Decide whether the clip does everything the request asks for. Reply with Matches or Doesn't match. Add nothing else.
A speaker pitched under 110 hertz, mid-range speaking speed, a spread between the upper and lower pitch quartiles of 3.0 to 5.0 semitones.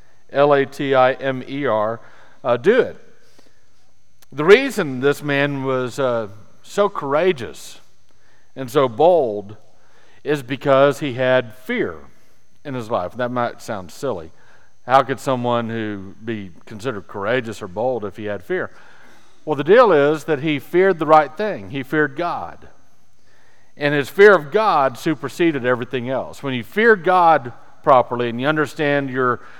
Doesn't match